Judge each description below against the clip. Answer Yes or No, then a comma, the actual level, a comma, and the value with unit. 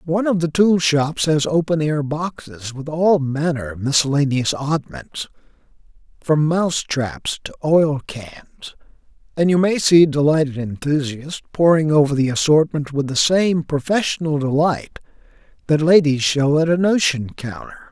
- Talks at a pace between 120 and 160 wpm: Yes, average, 145 wpm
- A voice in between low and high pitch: Yes, medium, 150 Hz